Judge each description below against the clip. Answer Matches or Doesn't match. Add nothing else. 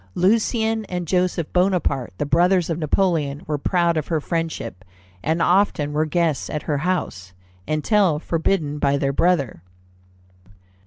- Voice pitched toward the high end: Doesn't match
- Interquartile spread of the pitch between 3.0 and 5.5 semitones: Matches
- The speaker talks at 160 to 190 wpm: Doesn't match